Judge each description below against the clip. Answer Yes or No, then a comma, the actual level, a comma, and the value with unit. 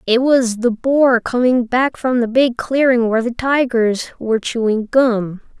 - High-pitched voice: Yes, high, 240 Hz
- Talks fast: No, average, 170 wpm